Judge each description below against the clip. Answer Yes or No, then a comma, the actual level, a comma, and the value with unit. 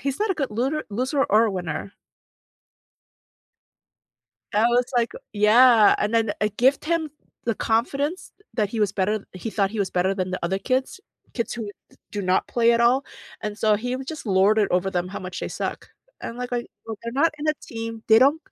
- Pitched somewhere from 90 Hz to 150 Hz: No, high, 225 Hz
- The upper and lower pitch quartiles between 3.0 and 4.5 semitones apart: Yes, average, 4.0 semitones